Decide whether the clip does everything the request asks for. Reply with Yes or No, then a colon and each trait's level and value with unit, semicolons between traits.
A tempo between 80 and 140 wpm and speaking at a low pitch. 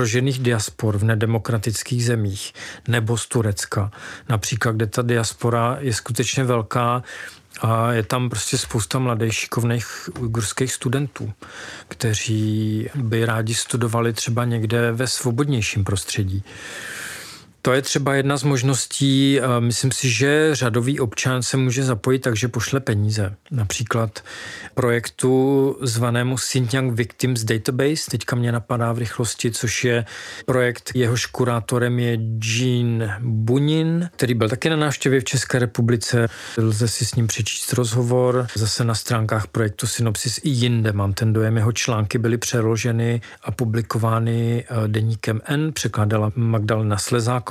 Yes: average, 130 wpm; low, 120 Hz